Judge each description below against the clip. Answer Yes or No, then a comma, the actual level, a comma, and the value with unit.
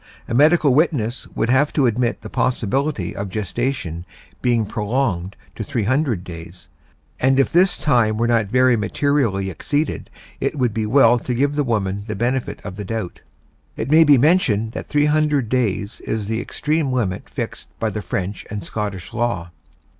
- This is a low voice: Yes, low, 120 Hz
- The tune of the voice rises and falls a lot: No, average, 5.0 semitones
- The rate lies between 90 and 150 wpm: No, average, 170 wpm